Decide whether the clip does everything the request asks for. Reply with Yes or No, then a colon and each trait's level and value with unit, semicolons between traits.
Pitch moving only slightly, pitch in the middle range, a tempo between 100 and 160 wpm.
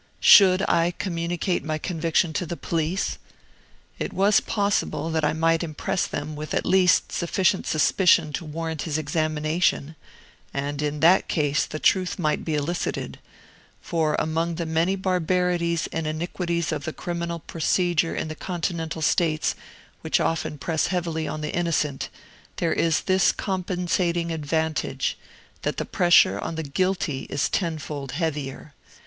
Yes: narrow, 2.3 semitones; medium, 165 Hz; average, 140 wpm